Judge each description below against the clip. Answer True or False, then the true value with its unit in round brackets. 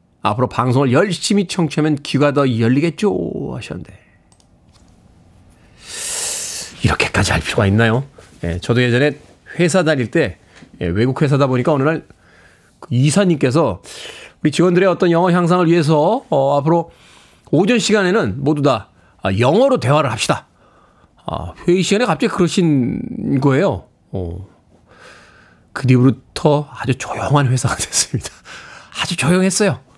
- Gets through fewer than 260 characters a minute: False (285 characters per minute)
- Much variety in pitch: True (7.0 semitones)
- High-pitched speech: False (145 Hz)